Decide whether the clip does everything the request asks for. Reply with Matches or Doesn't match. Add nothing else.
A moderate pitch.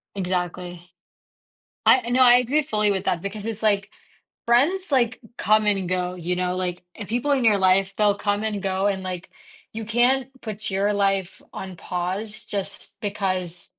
Doesn't match